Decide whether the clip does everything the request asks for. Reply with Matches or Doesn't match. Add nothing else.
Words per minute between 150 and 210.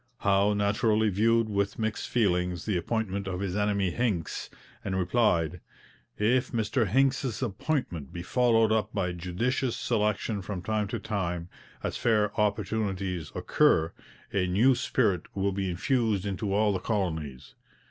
Doesn't match